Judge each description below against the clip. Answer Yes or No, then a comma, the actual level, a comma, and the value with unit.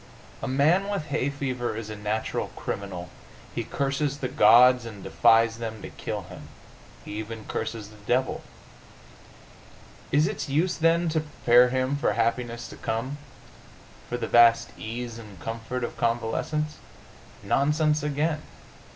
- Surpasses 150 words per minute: No, average, 140 wpm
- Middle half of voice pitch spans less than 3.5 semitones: No, average, 4.2 semitones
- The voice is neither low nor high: No, low, 125 Hz